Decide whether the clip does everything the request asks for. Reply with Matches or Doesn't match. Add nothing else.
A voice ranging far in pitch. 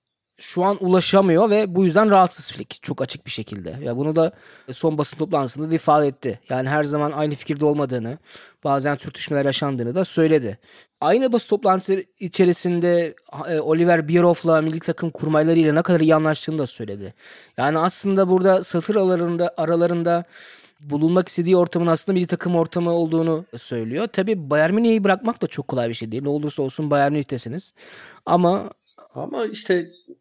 Doesn't match